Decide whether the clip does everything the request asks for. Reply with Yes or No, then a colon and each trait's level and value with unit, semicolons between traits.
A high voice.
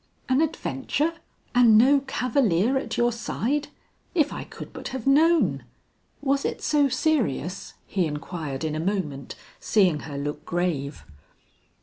Yes: high, 225 Hz